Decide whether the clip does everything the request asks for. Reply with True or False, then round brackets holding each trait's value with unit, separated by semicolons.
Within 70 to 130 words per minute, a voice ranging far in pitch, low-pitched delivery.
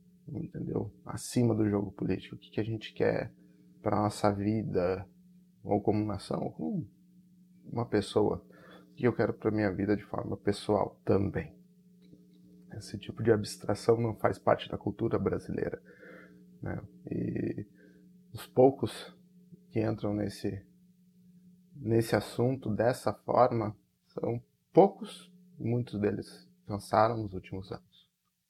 True (125 wpm; 7.2 semitones; 110 Hz)